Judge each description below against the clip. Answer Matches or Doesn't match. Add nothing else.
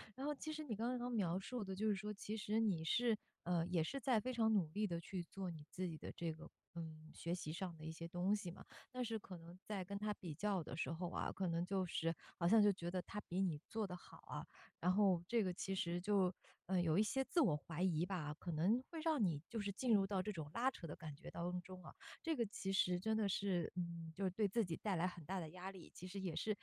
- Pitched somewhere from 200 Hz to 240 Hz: Doesn't match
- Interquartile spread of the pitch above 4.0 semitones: Doesn't match